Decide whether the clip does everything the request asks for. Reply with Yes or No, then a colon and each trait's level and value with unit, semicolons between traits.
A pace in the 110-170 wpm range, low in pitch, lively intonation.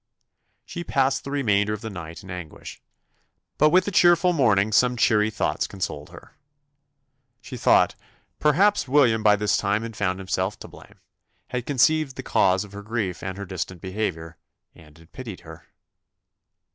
Yes: average, 165 wpm; low, 105 Hz; wide, 6.0 semitones